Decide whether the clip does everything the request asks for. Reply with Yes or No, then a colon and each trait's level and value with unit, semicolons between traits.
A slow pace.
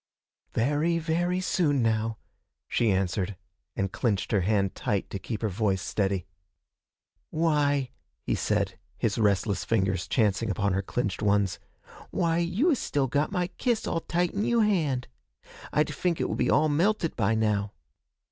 No: average, 155 wpm